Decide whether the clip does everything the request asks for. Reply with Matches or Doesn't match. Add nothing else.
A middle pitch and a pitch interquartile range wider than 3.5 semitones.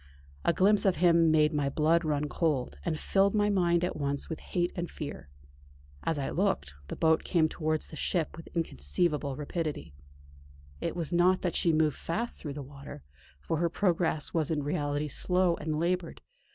Doesn't match